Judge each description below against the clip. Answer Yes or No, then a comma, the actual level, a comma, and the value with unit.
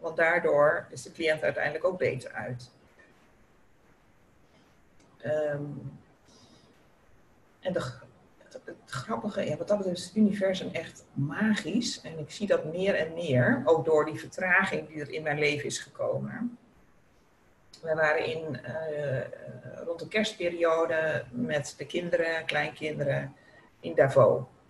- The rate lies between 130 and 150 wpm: Yes, slow, 135 wpm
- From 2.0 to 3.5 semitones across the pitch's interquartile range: Yes, average, 3.1 semitones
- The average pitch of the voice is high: No, medium, 160 Hz